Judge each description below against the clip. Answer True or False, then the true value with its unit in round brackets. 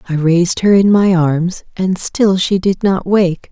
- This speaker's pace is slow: False (205 wpm)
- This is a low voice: False (185 Hz)